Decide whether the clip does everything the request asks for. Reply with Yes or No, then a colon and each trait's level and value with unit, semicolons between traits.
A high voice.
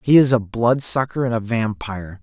No: low, 115 Hz